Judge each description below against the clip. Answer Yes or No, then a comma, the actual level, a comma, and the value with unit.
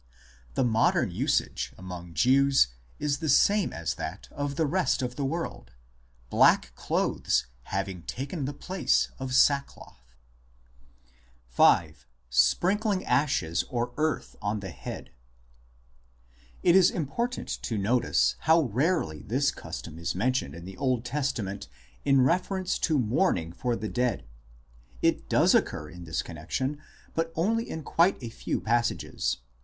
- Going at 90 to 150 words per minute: Yes, average, 140 wpm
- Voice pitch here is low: Yes, low, 130 Hz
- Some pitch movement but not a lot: No, wide, 8.6 semitones